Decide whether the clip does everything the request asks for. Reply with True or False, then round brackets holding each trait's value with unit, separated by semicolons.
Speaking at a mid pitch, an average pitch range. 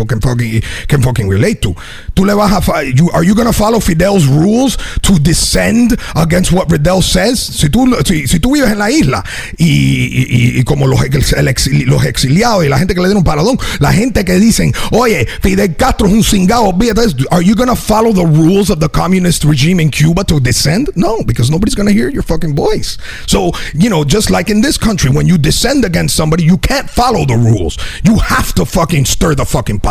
False (170 Hz; 6.6 semitones)